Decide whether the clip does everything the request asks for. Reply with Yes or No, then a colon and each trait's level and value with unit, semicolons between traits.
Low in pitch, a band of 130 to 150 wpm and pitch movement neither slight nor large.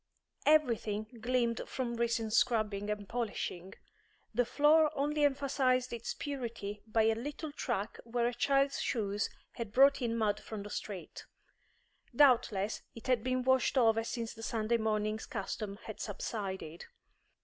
No: high, 230 Hz; average, 145 wpm; average, 3.2 semitones